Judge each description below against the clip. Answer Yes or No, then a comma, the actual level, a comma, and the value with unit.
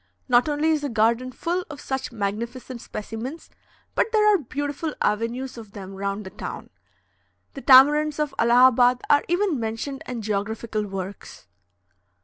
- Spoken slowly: No, average, 145 wpm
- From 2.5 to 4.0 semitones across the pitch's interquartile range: No, average, 4.8 semitones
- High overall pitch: Yes, very high, 250 Hz